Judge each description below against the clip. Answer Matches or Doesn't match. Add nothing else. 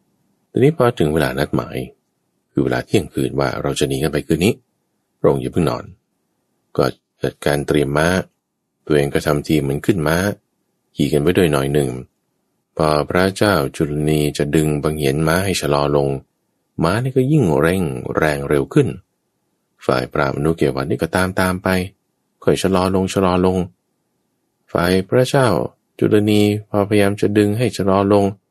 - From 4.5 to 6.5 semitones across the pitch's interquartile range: Matches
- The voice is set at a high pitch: Doesn't match